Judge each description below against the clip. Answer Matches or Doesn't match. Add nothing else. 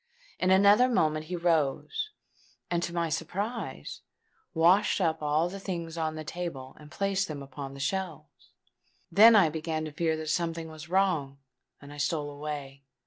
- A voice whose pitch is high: Doesn't match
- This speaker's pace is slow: Doesn't match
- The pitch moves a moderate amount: Matches